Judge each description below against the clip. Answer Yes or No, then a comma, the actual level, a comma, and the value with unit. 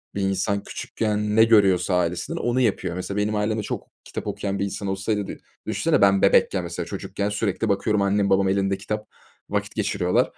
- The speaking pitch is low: Yes, low, 100 Hz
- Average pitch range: No, narrow, 1.5 semitones